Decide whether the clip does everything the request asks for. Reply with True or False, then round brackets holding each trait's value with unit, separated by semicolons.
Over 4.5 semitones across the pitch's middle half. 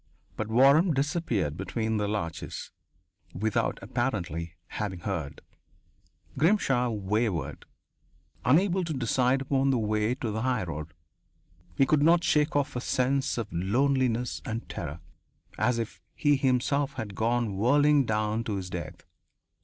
True (5.2 semitones)